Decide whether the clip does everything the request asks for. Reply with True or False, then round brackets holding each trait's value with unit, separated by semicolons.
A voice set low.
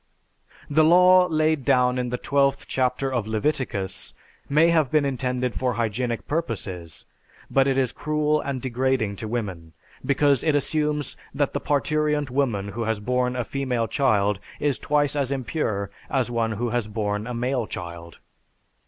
True (125 Hz)